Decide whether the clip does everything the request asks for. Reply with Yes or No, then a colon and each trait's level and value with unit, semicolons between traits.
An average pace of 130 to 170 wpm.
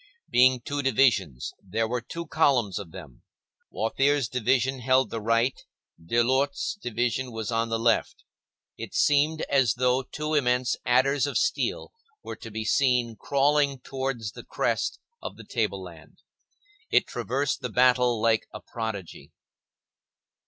Yes: average, 140 wpm